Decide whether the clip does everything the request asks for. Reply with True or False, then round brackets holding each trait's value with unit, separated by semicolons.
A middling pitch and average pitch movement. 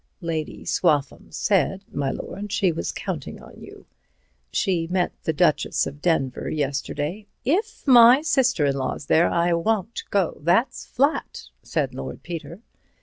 False (175 Hz; 6.2 semitones)